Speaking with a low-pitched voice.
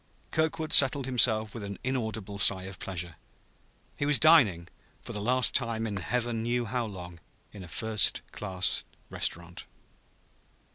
Yes: low, 110 Hz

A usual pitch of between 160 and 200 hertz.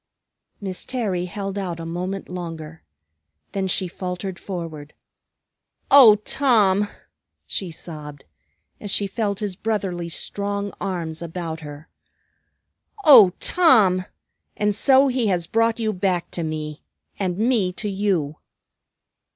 Yes: high, 190 Hz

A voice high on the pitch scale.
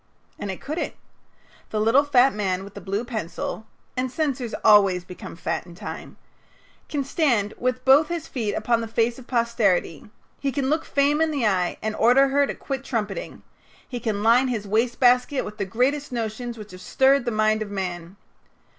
Yes: high, 235 Hz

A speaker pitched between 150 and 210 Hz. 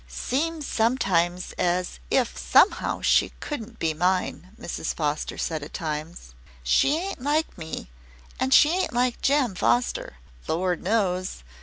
Yes: medium, 185 Hz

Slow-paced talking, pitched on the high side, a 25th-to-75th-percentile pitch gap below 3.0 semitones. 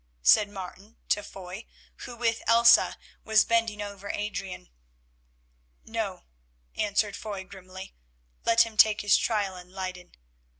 Yes: slow, 125 wpm; high, 205 Hz; narrow, 2.5 semitones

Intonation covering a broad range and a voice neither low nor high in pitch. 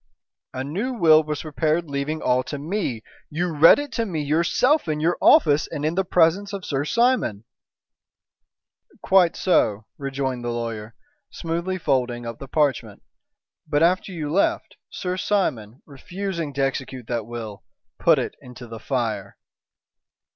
Yes: wide, 5.8 semitones; medium, 150 Hz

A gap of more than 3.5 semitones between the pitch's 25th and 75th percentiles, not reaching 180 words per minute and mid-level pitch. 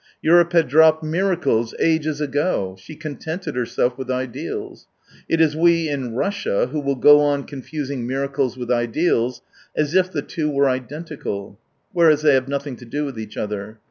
Yes: average, 4.0 semitones; average, 170 wpm; medium, 145 Hz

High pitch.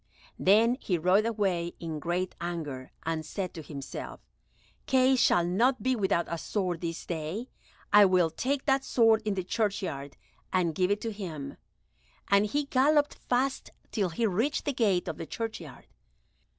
Yes: high, 195 Hz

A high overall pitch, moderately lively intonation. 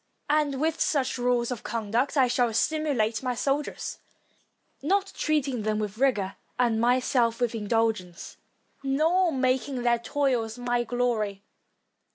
Yes: high, 245 Hz; average, 3.3 semitones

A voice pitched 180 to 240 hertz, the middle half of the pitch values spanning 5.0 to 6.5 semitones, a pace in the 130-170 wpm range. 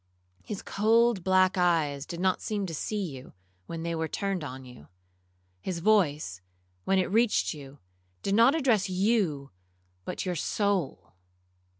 Yes: medium, 185 Hz; average, 5.3 semitones; average, 150 wpm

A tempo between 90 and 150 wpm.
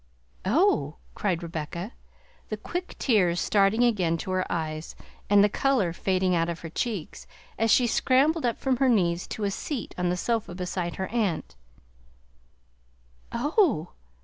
No: average, 160 wpm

